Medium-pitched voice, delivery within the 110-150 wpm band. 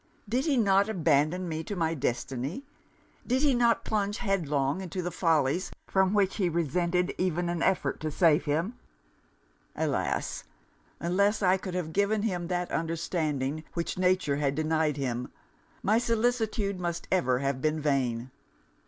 Yes: medium, 175 Hz; average, 145 wpm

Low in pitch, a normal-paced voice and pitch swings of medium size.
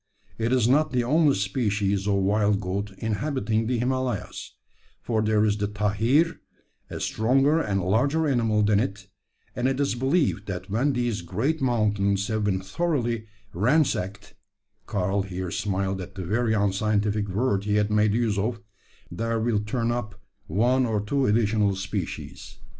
Yes: low, 105 Hz; average, 155 wpm; average, 3.4 semitones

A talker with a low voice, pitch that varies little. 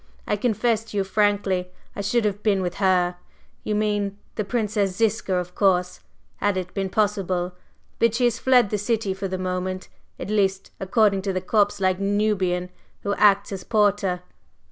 No: high, 200 Hz; narrow, 2.1 semitones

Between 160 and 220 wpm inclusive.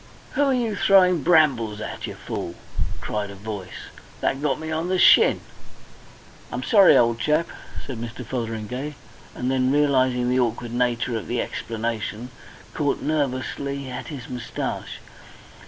No: average, 145 wpm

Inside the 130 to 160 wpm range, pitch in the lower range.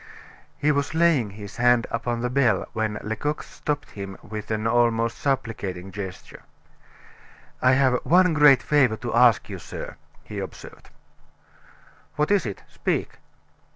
Yes: average, 140 wpm; low, 120 Hz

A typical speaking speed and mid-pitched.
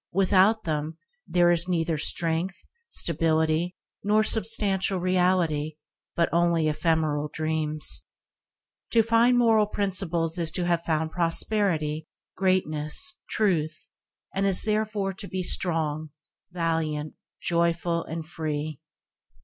No: slow, 110 wpm; medium, 170 Hz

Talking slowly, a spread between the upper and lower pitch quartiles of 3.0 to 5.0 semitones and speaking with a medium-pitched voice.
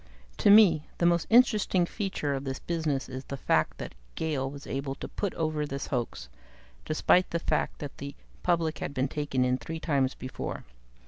No: average, 185 wpm; average, 4.1 semitones; medium, 150 Hz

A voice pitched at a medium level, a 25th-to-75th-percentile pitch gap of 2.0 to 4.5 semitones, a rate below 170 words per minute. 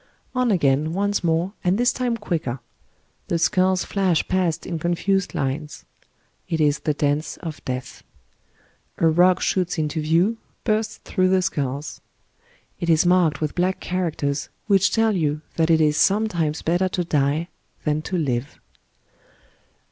Yes: medium, 170 Hz; average, 3.7 semitones; average, 150 wpm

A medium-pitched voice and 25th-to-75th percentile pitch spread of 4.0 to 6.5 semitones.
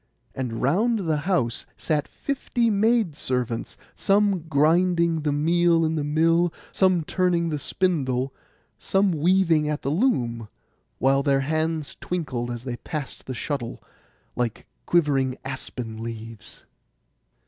Yes: medium, 155 Hz; average, 5.1 semitones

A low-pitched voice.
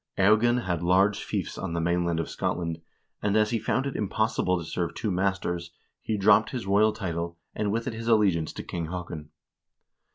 Yes: very low, 95 Hz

